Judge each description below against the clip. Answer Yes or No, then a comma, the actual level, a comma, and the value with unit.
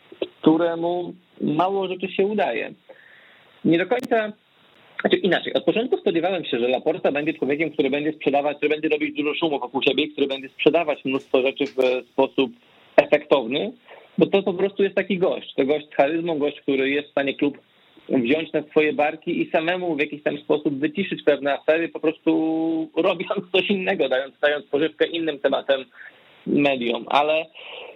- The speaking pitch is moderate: Yes, medium, 155 Hz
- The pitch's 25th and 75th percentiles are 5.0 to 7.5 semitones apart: No, average, 3.4 semitones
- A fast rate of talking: Yes, fast, 165 wpm